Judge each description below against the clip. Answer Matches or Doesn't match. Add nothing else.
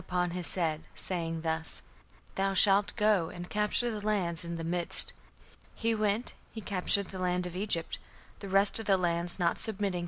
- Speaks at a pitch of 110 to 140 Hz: Doesn't match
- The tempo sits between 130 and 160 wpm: Doesn't match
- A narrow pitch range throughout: Doesn't match